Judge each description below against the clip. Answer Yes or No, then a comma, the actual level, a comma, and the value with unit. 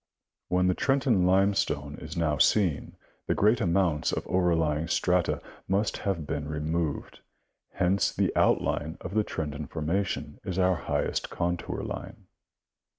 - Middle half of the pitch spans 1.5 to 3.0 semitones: No, average, 3.8 semitones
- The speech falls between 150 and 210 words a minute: No, slow, 135 wpm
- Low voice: Yes, very low, 90 Hz